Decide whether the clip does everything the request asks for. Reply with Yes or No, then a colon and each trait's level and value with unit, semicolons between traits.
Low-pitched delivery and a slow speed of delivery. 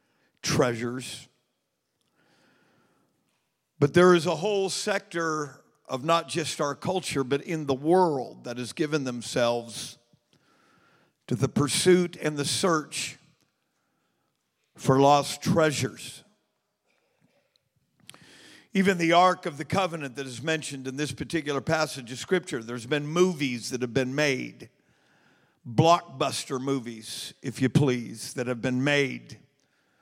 No: medium, 145 Hz; slow, 120 wpm